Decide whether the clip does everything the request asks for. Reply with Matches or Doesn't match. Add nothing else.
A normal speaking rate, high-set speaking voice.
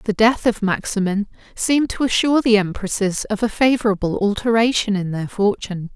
Matches